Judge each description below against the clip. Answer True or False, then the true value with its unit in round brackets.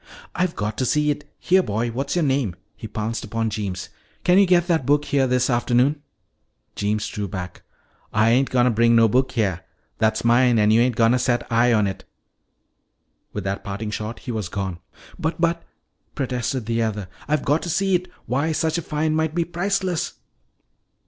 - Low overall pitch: True (125 Hz)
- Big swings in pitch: True (5.7 semitones)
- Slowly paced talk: False (190 wpm)